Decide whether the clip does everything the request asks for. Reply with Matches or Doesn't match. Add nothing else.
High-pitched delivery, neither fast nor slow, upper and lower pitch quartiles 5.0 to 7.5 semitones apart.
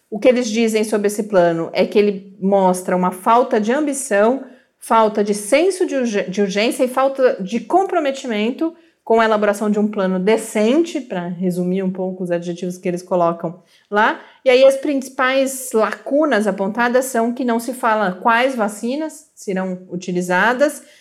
Matches